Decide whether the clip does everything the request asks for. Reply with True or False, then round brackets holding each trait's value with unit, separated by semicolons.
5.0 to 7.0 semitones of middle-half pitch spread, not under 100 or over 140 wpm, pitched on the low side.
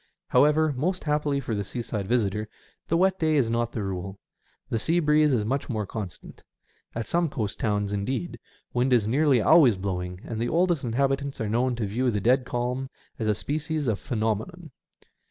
False (5.5 semitones; 185 wpm; 120 Hz)